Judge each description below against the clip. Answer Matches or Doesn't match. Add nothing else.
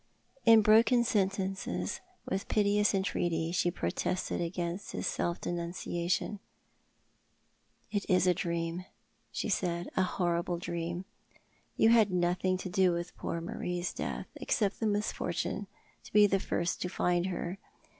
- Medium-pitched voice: Matches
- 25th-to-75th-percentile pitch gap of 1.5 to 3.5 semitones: Matches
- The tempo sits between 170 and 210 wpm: Doesn't match